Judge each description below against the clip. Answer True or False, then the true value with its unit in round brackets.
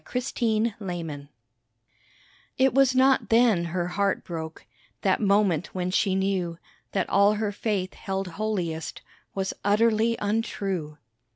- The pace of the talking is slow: True (125 wpm)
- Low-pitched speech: False (200 Hz)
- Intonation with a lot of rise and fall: False (3.6 semitones)